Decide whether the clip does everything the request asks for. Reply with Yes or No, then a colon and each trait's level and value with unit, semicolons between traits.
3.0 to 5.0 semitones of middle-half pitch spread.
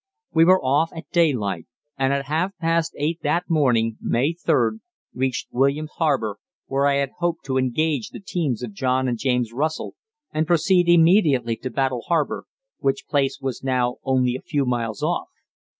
Yes: average, 4.4 semitones